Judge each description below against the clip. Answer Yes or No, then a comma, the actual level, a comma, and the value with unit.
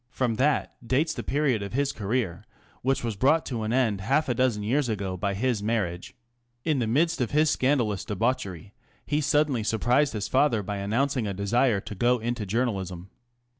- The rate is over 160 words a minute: Yes, average, 185 wpm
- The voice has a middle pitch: No, low, 120 Hz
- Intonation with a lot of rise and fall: No, average, 4.7 semitones